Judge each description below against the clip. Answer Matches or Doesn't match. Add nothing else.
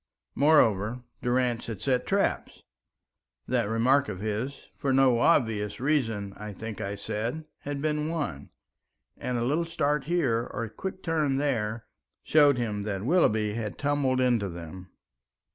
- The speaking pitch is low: Matches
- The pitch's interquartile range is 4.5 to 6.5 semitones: Matches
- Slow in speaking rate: Doesn't match